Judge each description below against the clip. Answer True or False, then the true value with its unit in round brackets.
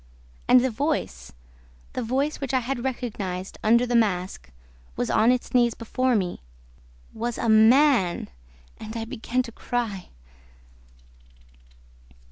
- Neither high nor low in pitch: False (235 Hz)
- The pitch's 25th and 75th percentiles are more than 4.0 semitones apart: False (2.9 semitones)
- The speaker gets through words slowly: True (125 wpm)